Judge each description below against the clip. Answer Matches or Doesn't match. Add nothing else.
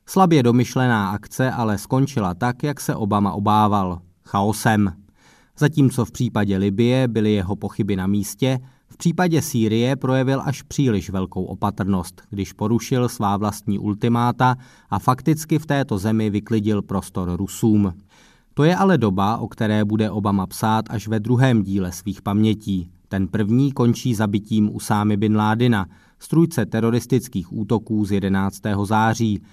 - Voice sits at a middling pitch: Doesn't match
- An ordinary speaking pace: Matches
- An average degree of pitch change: Matches